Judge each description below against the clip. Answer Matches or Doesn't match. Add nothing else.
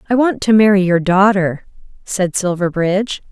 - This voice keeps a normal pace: Matches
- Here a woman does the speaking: Matches